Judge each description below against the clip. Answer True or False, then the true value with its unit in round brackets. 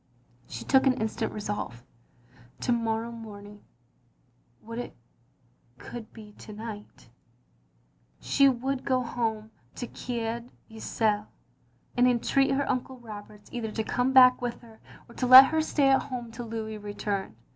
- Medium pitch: False (230 Hz)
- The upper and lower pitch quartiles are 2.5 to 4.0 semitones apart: True (3.0 semitones)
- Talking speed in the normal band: True (155 wpm)